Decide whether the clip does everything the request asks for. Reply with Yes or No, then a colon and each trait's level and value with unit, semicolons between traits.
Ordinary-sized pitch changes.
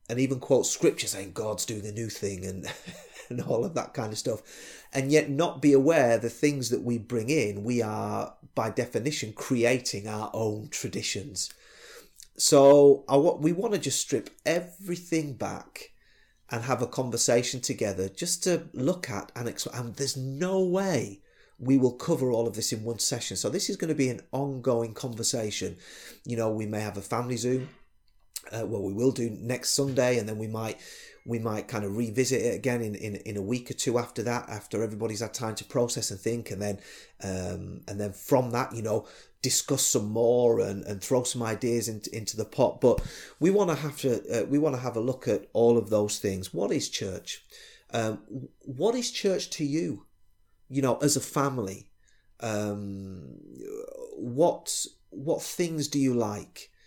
Yes: average, 4.4 semitones